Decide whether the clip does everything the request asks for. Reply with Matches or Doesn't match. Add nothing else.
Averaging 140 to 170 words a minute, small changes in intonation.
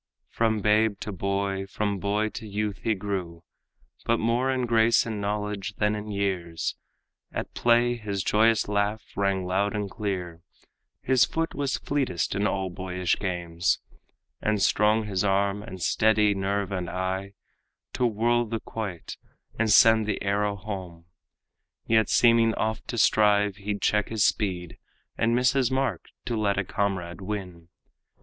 Matches